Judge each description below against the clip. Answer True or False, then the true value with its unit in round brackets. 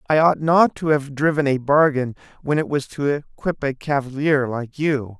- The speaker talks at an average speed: True (195 wpm)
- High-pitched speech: False (140 Hz)